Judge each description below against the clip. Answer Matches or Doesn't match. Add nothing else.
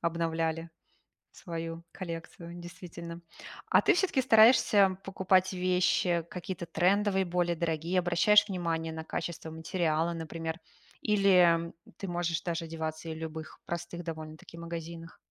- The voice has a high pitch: Doesn't match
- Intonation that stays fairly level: Matches